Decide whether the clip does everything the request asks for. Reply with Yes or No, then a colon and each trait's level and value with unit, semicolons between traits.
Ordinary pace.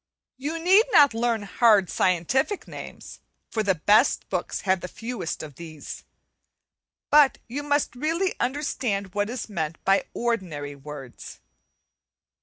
No: slow, 130 wpm